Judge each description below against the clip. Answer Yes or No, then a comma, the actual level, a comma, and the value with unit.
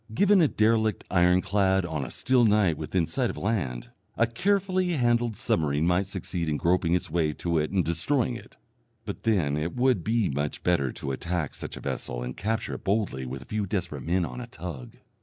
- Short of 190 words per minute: No, average, 200 wpm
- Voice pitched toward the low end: Yes, very low, 90 Hz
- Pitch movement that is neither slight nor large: No, wide, 6.0 semitones